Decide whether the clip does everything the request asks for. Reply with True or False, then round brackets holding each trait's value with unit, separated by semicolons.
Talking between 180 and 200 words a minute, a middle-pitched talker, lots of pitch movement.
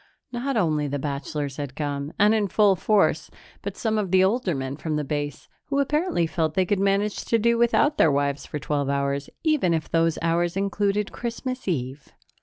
True (190 wpm; 175 Hz; 6.6 semitones)